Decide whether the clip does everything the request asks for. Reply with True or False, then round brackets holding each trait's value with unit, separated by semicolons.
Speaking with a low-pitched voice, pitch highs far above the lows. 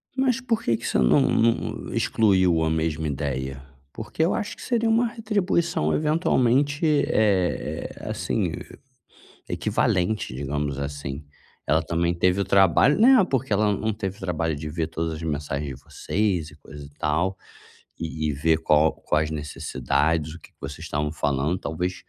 True (85 Hz; 6.7 semitones)